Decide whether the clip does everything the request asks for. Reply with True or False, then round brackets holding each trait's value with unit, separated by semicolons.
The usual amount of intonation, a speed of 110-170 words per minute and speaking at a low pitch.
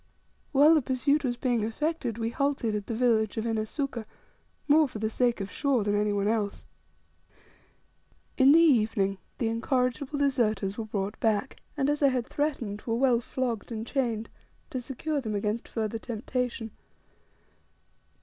False (3.8 semitones; 160 wpm; 235 Hz)